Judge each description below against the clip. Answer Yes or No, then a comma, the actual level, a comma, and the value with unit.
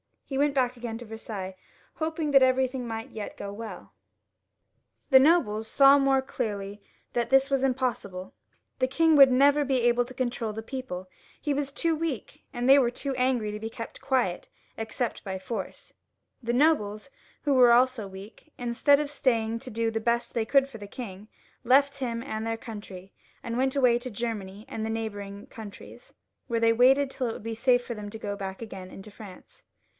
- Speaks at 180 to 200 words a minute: Yes, average, 190 wpm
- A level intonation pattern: No, average, 3.6 semitones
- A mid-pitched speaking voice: No, high, 235 Hz